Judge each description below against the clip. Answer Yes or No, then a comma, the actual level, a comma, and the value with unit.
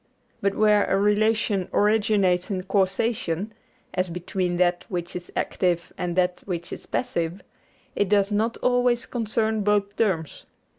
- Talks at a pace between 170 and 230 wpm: No, average, 140 wpm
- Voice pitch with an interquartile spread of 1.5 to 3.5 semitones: Yes, average, 3.1 semitones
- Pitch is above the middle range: Yes, high, 200 Hz